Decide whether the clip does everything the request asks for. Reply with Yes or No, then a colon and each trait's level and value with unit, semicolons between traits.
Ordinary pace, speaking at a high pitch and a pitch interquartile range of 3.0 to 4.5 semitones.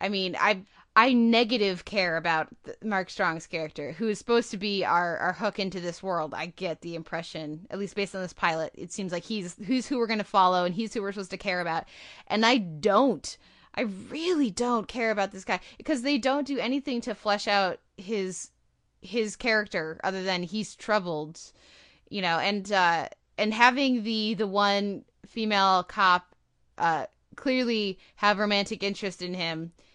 Yes: average, 180 wpm; high, 200 Hz; average, 3.6 semitones